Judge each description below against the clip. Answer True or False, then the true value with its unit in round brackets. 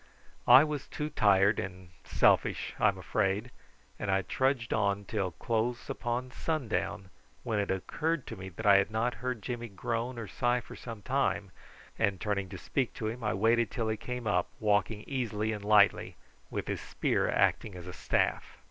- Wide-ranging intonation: False (3.5 semitones)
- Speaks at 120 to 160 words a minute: False (180 wpm)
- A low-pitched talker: True (110 Hz)